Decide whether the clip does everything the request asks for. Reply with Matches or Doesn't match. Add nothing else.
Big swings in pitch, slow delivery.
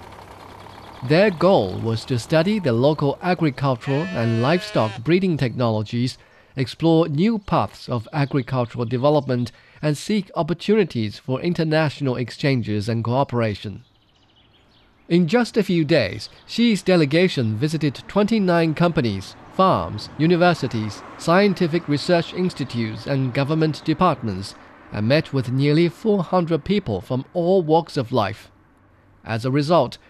Matches